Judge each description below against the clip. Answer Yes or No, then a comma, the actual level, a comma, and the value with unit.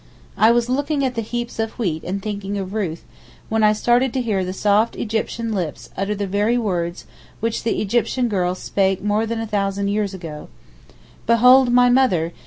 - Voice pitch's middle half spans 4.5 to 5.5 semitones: No, average, 3.4 semitones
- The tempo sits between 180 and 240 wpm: Yes, average, 190 wpm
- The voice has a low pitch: No, high, 210 Hz